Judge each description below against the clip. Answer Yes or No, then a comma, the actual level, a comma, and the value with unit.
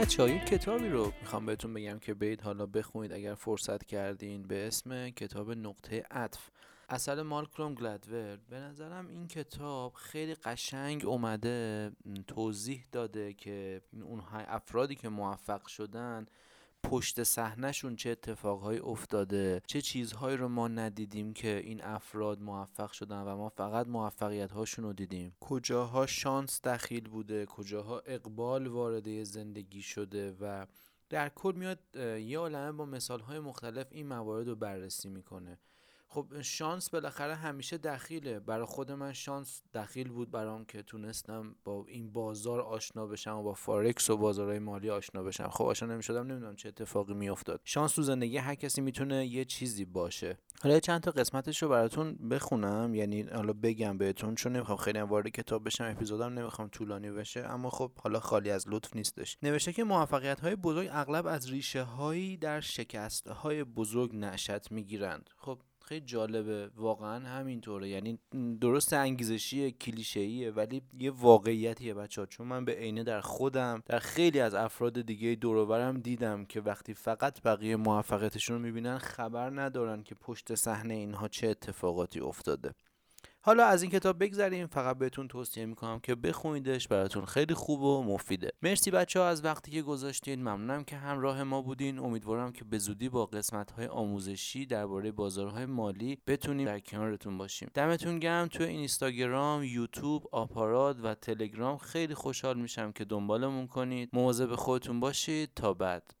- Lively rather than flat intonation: No, average, 4.1 semitones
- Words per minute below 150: No, fast, 155 wpm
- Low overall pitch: Yes, low, 115 Hz